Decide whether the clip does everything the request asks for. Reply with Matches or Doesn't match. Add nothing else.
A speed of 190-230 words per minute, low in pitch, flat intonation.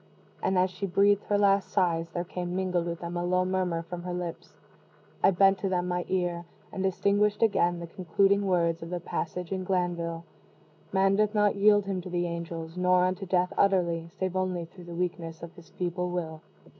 Doesn't match